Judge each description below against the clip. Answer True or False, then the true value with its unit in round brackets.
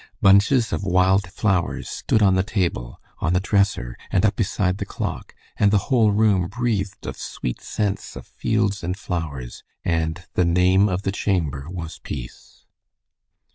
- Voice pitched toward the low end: True (95 Hz)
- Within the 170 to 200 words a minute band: False (160 wpm)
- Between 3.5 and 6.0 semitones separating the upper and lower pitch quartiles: False (2.9 semitones)